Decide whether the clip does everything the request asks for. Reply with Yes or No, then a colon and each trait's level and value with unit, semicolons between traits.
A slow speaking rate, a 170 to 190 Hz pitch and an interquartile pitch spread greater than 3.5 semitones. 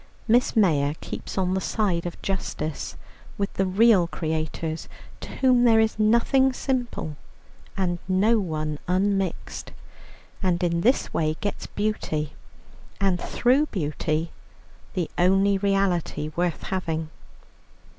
Yes: slow, 120 wpm; medium, 185 Hz; average, 4.6 semitones